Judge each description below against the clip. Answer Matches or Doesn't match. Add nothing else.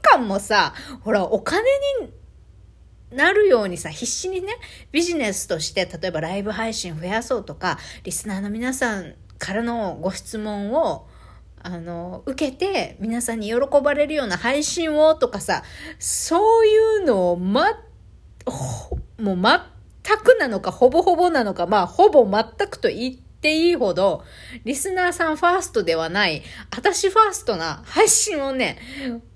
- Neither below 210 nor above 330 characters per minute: Matches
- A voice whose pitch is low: Doesn't match